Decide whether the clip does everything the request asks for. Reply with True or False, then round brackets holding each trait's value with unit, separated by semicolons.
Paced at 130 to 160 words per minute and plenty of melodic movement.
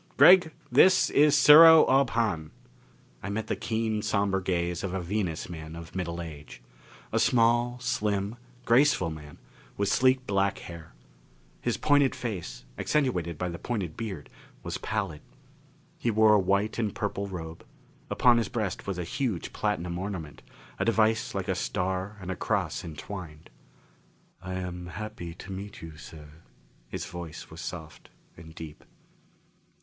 False (150 wpm; 4.9 semitones)